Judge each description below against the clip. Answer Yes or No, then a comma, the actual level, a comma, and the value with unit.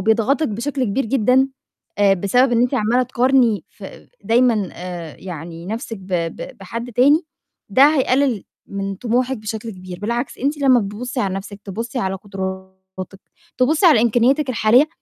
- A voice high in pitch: Yes, high, 230 Hz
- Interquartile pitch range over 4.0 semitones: Yes, average, 4.6 semitones